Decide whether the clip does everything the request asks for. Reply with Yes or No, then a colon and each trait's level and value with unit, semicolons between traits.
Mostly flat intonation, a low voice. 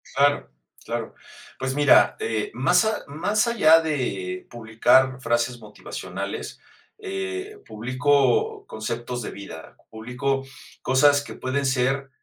No: average, 3.8 semitones; low, 130 Hz